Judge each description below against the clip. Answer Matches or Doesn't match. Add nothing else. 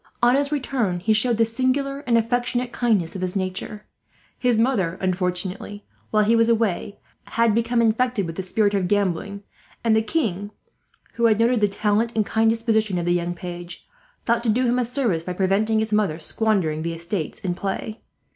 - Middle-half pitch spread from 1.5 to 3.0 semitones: Doesn't match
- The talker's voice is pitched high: Matches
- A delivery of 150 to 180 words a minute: Doesn't match